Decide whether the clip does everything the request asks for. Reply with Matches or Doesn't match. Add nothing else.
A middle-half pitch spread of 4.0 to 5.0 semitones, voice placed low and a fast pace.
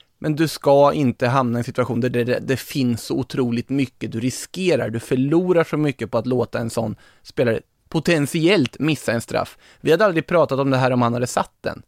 Matches